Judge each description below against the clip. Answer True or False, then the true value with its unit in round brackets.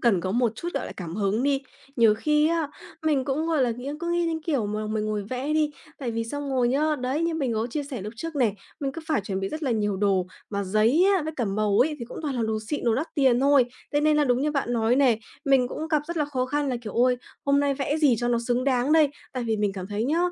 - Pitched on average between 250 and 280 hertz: True (255 Hz)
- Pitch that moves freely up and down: False (5.0 semitones)